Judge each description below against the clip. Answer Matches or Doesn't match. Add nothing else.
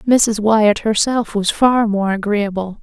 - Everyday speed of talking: Matches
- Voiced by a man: Doesn't match